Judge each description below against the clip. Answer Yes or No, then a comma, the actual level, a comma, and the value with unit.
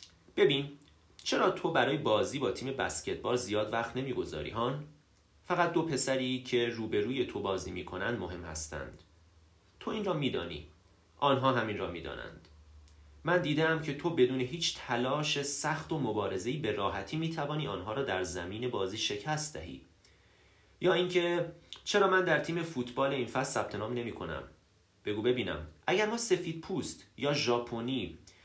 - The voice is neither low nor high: No, low, 120 Hz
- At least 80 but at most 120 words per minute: No, average, 150 wpm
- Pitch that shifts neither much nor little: No, wide, 8.5 semitones